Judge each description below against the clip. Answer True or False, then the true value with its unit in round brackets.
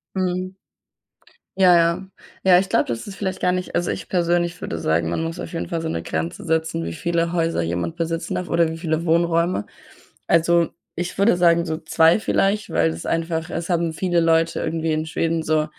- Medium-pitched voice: True (165 Hz)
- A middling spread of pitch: False (1.7 semitones)